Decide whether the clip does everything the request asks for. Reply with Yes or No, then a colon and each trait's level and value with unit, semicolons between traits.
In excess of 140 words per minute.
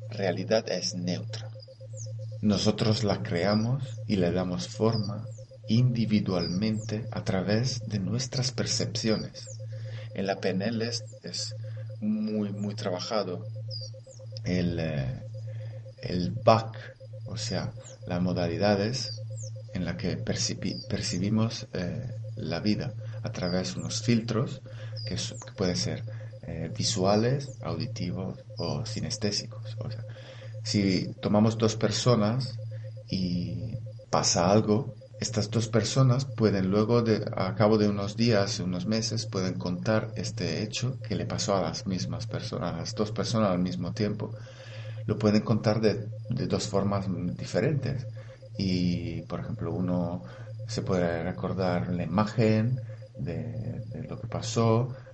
No: slow, 125 wpm